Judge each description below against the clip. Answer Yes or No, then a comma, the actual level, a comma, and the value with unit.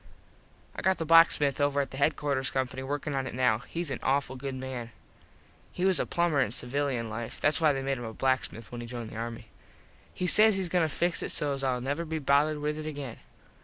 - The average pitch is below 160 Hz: Yes, medium, 140 Hz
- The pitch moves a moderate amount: Yes, average, 3.3 semitones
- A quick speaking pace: Yes, fast, 225 wpm